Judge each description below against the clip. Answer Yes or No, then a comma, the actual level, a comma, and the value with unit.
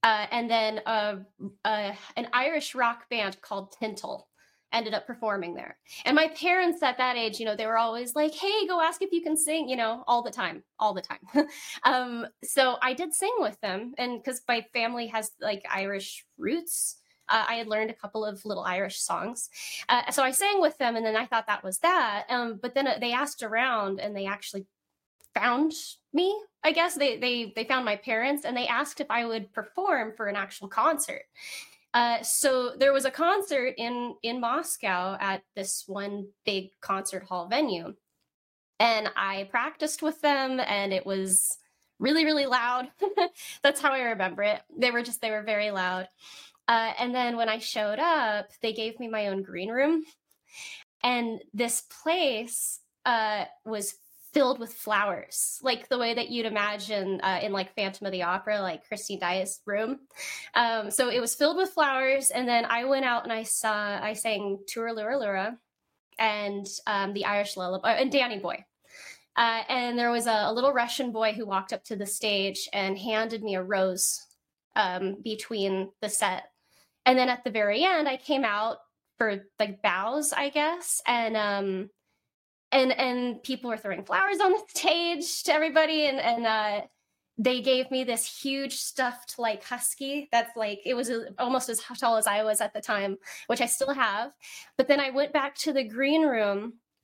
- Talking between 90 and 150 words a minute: No, average, 190 wpm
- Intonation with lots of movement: No, average, 4.5 semitones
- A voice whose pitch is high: Yes, high, 235 Hz